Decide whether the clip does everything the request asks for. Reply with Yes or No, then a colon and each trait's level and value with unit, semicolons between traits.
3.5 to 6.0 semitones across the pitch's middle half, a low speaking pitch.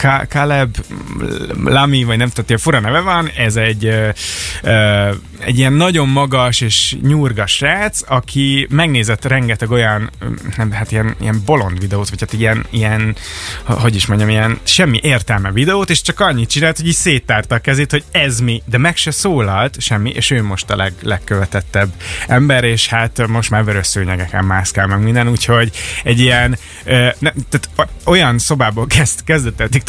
Yes: average, 4.4 semitones; low, 115 Hz